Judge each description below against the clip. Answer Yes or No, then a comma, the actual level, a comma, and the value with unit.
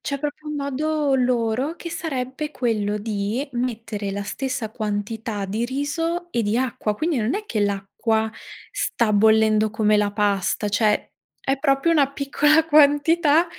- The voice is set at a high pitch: Yes, high, 245 Hz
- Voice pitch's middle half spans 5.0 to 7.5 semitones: Yes, wide, 5.5 semitones